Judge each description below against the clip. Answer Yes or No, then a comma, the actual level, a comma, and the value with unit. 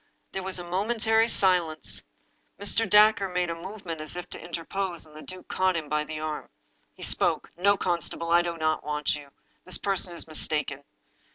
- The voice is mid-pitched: Yes, medium, 175 Hz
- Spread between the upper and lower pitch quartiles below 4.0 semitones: Yes, average, 3.6 semitones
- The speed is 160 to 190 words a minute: Yes, average, 185 wpm